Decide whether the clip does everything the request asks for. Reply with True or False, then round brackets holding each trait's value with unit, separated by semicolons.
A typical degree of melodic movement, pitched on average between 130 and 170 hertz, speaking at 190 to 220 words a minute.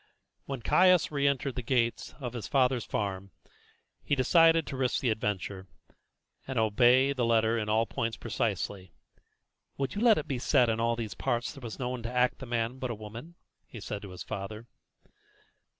False (3.2 semitones; 120 Hz; 200 wpm)